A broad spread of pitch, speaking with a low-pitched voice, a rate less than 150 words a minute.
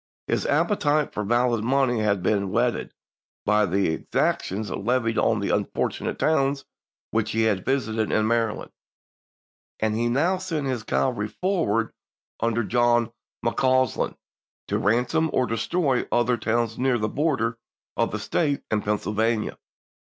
No: average, 3.4 semitones; low, 115 Hz; average, 140 wpm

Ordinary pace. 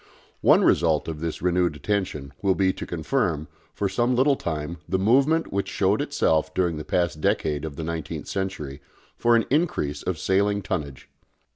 Yes: average, 170 wpm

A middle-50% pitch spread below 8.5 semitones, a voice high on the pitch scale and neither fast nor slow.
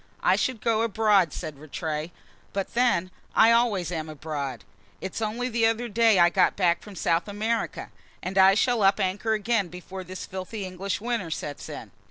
Yes: average, 4.3 semitones; high, 195 Hz; average, 180 wpm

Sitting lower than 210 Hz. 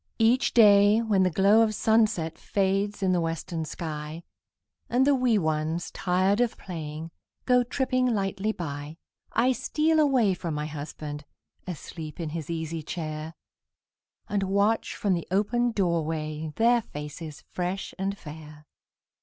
Yes: medium, 185 Hz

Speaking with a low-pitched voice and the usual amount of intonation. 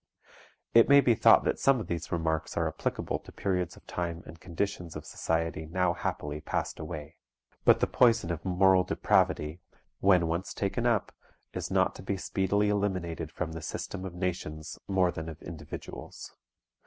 Yes: very low, 90 Hz; average, 3.0 semitones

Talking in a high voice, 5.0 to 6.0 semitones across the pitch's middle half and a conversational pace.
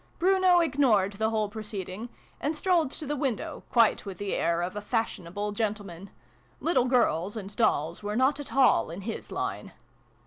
Yes: high, 215 Hz; wide, 5.4 semitones; average, 170 wpm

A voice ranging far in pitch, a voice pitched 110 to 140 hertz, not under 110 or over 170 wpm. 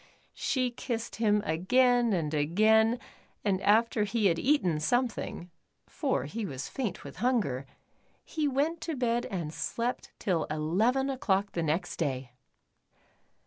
No: wide, 6.7 semitones; high, 210 Hz; average, 140 wpm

